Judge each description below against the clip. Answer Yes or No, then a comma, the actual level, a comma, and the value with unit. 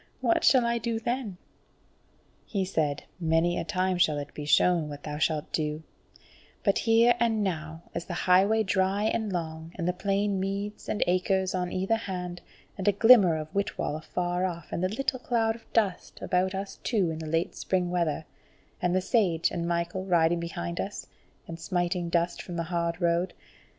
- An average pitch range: Yes, average, 3.1 semitones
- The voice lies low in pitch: No, medium, 180 Hz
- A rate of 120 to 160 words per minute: No, average, 185 wpm